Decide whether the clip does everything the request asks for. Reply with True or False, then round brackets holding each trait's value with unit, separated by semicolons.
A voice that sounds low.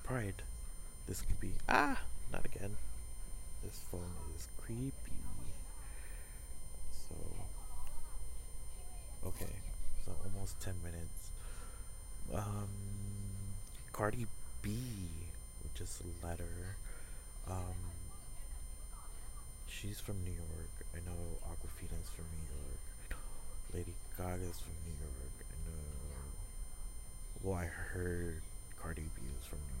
True (85 Hz)